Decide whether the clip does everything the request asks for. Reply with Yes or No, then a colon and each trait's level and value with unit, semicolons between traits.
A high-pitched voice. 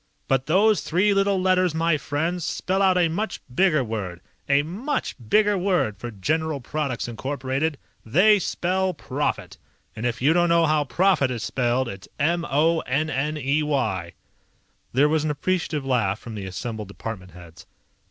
No: medium, 150 Hz